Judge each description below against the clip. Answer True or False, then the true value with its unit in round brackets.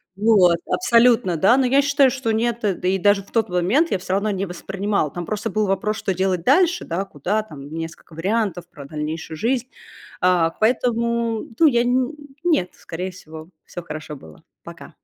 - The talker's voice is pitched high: True (195 Hz)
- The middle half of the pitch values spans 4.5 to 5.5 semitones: True (5.1 semitones)